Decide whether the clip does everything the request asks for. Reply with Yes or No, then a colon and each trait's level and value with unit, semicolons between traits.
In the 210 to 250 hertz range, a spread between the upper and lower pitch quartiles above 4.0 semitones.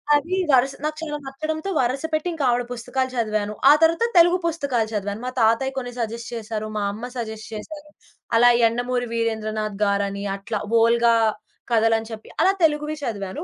Yes: high, 235 Hz; average, 4.6 semitones